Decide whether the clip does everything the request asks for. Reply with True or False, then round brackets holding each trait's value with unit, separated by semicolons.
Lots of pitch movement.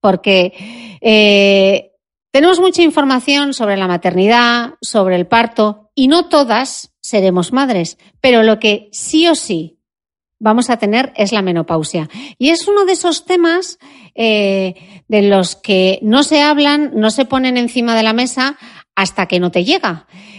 True (5.8 semitones)